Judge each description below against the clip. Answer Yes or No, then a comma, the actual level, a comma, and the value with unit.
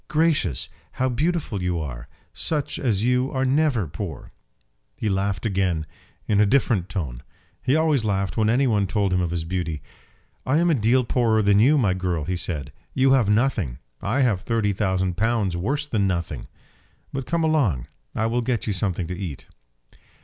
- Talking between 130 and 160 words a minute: No, average, 185 wpm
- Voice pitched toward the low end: Yes, low, 105 Hz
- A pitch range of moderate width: No, wide, 6.2 semitones